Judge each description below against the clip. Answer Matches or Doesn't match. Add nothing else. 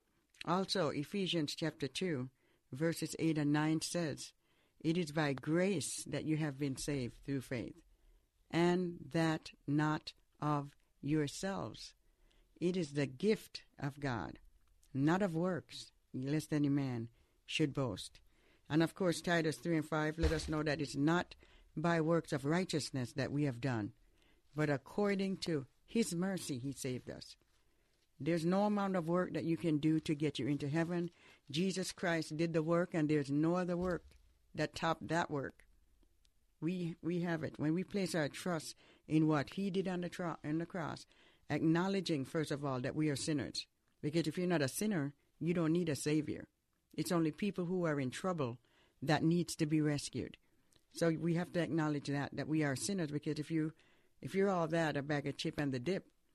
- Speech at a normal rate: Matches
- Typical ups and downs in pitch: Matches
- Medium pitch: Matches